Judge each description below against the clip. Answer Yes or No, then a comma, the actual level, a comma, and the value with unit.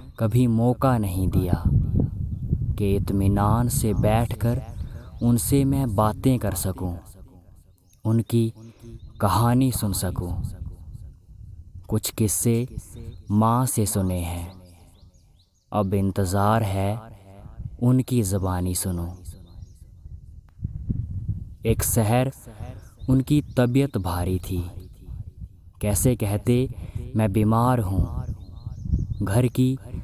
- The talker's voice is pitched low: Yes, low, 105 Hz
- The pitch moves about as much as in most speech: Yes, average, 4.1 semitones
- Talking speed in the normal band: No, slow, 85 wpm